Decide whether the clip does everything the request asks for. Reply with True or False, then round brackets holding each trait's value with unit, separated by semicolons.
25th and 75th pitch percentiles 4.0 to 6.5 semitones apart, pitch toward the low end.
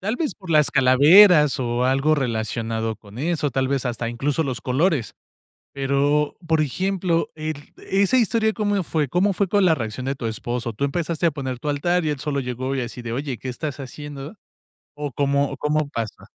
False (4.4 semitones; 145 Hz)